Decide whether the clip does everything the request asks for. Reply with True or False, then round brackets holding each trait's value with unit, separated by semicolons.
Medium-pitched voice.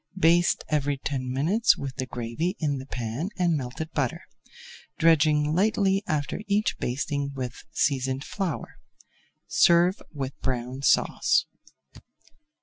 True (145 Hz)